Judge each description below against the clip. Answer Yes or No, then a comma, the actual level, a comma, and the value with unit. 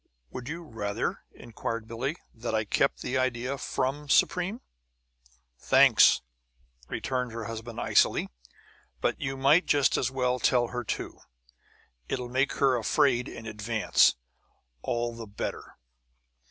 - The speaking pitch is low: Yes, low, 125 Hz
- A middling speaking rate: No, slow, 125 wpm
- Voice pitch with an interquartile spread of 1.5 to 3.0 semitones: Yes, average, 2.7 semitones